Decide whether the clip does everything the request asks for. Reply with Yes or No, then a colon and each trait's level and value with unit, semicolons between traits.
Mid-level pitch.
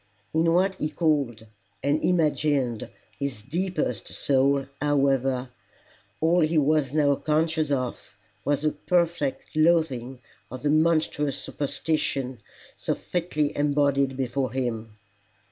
Yes: medium, 145 Hz